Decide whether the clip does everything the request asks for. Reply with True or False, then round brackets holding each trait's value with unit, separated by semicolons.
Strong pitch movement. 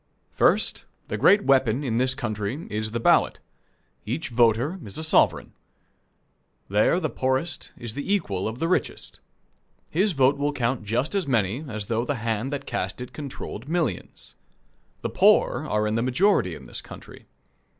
False (5.0 semitones)